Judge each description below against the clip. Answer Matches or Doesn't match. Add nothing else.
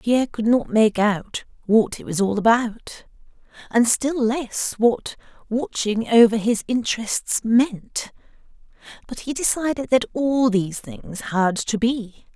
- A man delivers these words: Doesn't match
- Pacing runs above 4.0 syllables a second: Doesn't match